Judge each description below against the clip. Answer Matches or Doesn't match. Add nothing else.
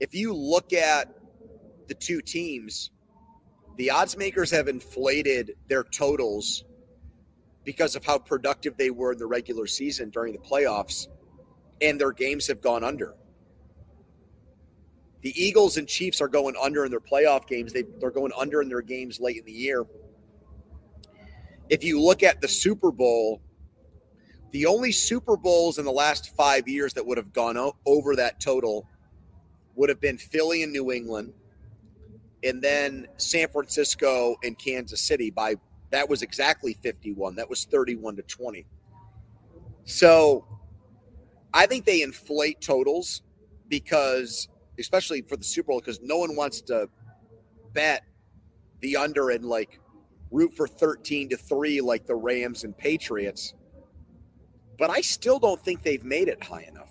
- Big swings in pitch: Matches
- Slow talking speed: Doesn't match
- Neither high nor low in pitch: Doesn't match